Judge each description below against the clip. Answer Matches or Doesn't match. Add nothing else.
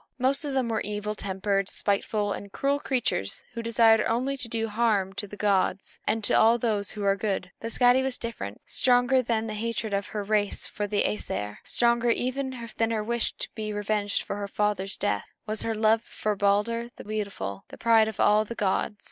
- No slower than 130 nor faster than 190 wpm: Doesn't match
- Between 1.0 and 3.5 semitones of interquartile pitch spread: Matches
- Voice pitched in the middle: Doesn't match